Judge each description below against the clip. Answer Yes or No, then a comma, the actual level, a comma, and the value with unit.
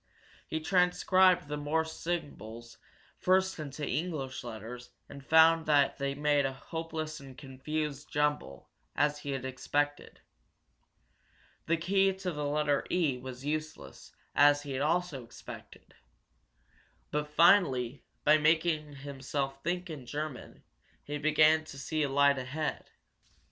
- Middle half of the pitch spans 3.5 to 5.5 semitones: No, average, 2.7 semitones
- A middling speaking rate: No, slow, 130 wpm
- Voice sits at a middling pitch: Yes, medium, 150 Hz